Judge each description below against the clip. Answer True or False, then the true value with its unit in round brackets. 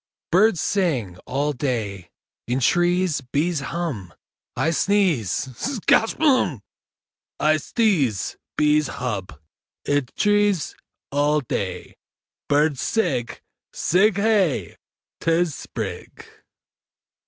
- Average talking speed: False (90 wpm)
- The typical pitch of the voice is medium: True (150 Hz)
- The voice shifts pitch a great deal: True (6.5 semitones)